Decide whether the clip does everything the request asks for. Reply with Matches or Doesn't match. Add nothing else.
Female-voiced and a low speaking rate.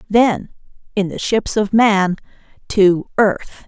Matches